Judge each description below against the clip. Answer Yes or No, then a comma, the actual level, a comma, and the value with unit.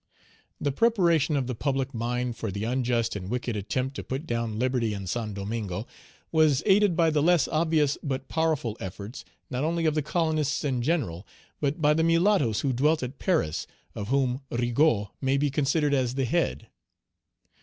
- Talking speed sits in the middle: Yes, average, 175 wpm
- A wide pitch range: No, average, 5.0 semitones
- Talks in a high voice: No, low, 135 Hz